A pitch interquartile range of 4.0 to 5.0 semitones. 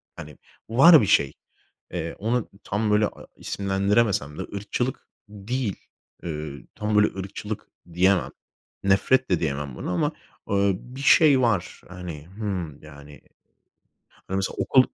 Yes: average, 4.5 semitones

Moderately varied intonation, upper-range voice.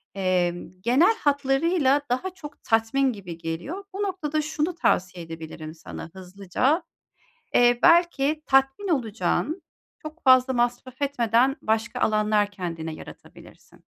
No: wide, 7.2 semitones; very high, 255 Hz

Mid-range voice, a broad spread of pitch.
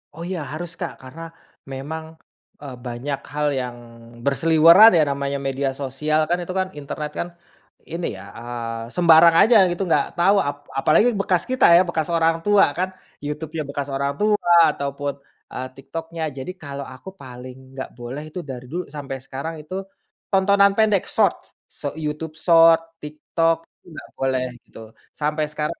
No: medium, 150 Hz; average, 3.7 semitones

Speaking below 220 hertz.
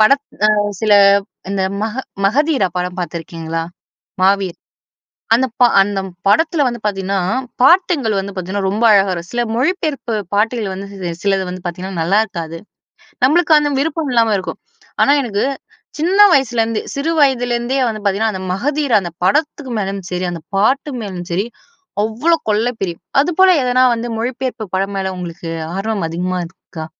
Yes: high, 210 Hz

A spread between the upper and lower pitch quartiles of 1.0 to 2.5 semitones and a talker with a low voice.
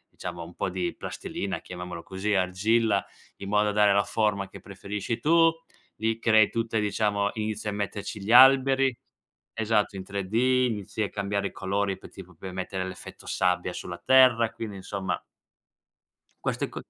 No: average, 2.9 semitones; low, 100 Hz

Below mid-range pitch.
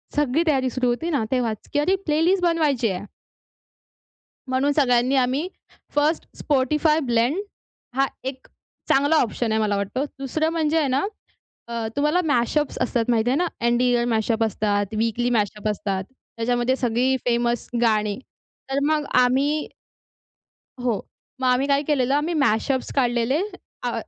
No: very high, 255 Hz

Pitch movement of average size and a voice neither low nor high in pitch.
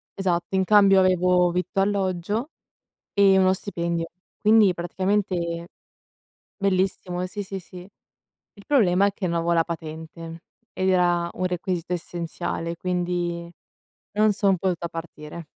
No: narrow, 2.2 semitones; medium, 180 Hz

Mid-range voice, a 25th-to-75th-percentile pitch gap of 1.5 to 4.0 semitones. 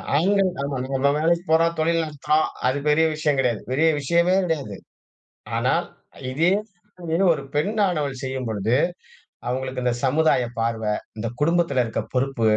No: medium, 150 Hz; average, 4.4 semitones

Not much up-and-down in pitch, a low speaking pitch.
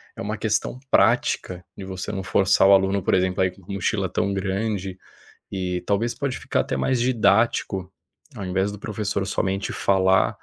Yes: narrow, 1.8 semitones; very low, 95 Hz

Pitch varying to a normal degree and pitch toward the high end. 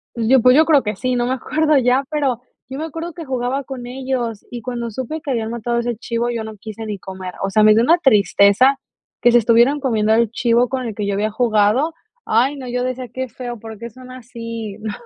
Yes: average, 3.0 semitones; high, 240 Hz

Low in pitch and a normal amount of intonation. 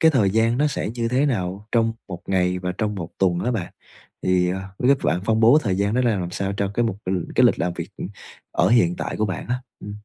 Yes: low, 100 Hz; average, 4.3 semitones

